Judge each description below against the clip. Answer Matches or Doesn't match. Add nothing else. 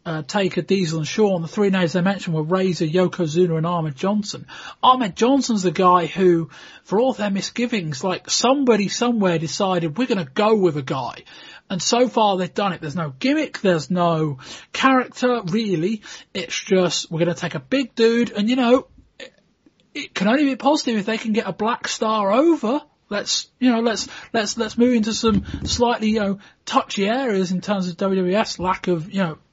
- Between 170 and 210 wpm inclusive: Matches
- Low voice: Doesn't match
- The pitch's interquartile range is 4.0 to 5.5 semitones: Matches